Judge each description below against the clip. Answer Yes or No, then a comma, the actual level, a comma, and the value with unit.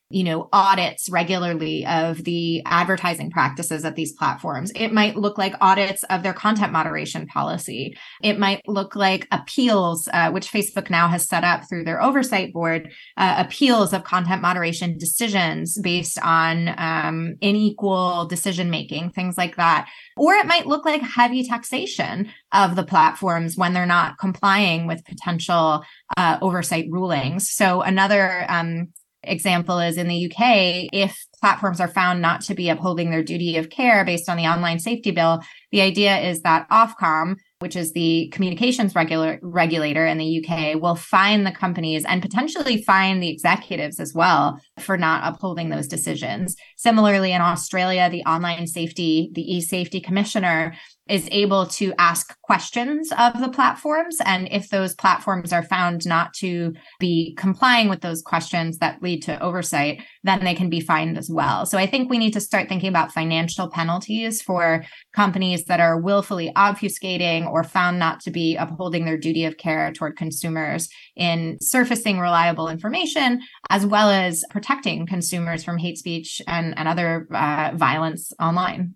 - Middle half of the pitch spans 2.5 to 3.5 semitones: Yes, average, 2.9 semitones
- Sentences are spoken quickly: Yes, fast, 165 wpm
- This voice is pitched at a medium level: Yes, medium, 180 Hz